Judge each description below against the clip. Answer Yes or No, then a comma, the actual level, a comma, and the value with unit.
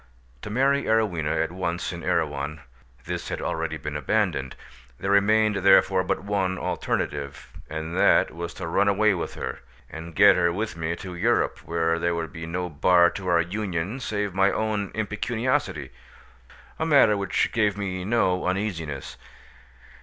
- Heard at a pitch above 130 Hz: No, very low, 90 Hz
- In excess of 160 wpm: No, average, 155 wpm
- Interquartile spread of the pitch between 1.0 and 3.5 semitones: No, average, 3.9 semitones